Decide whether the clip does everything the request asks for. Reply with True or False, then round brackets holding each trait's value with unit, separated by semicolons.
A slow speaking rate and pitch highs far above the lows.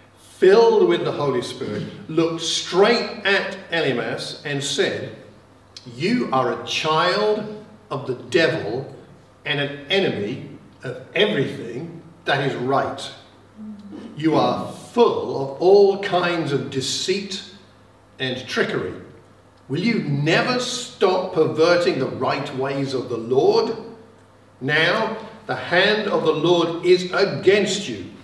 True (120 wpm; 7.3 semitones)